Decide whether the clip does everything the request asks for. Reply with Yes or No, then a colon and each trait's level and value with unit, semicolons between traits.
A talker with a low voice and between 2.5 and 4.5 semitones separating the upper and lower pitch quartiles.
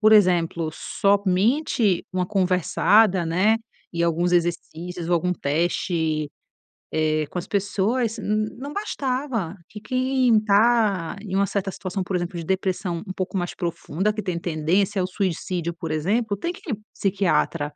No: medium, 185 Hz; average, 3.7 semitones